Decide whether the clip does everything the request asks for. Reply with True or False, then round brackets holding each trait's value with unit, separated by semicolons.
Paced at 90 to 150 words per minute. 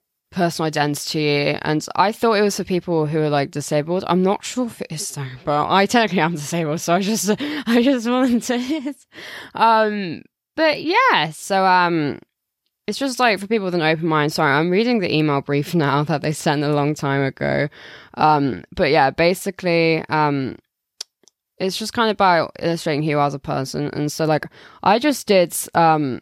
False (190 wpm)